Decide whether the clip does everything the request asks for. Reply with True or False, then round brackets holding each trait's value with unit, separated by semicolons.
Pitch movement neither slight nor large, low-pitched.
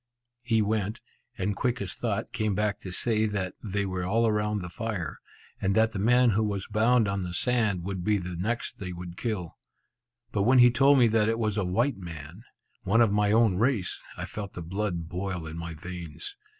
True (3.5 semitones; 105 Hz)